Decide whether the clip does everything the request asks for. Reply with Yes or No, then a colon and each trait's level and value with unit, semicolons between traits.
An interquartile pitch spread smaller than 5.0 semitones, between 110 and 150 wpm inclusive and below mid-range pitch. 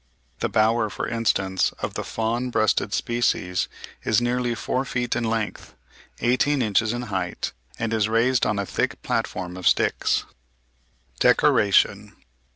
Yes: average, 2.9 semitones; average, 140 wpm; low, 115 Hz